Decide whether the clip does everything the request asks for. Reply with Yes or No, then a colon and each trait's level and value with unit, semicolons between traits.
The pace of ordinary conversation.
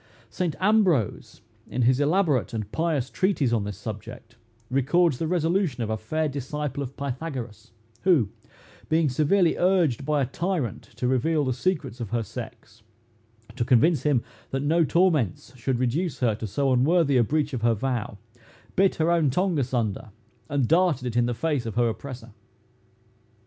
Yes: average, 165 wpm